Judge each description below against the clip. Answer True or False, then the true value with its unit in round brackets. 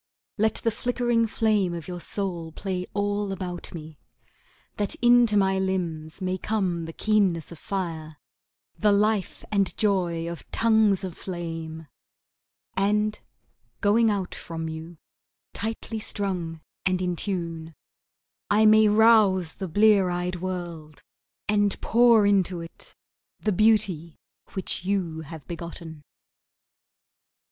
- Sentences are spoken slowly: True (120 wpm)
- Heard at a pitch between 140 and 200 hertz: True (190 Hz)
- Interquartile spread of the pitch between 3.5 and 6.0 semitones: True (3.8 semitones)